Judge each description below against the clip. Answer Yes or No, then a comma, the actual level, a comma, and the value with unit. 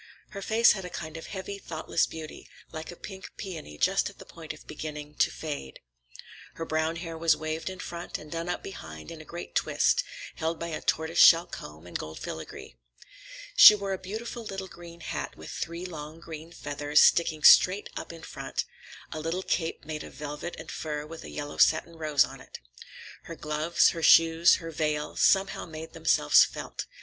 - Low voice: No, medium, 165 Hz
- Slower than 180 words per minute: No, average, 190 wpm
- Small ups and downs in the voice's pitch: Yes, narrow, 2.2 semitones